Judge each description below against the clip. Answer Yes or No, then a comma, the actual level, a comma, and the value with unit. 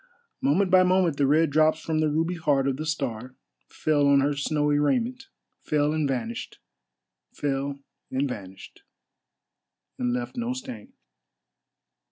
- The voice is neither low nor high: Yes, medium, 145 Hz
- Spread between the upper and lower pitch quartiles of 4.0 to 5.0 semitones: No, average, 2.9 semitones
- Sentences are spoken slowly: Yes, slow, 130 wpm